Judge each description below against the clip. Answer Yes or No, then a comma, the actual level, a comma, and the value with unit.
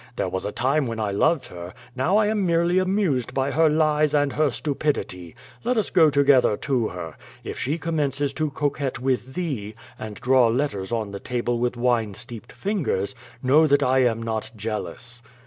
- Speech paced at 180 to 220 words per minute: Yes, average, 185 wpm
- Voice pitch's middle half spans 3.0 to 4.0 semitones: No, average, 5.1 semitones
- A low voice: Yes, low, 130 Hz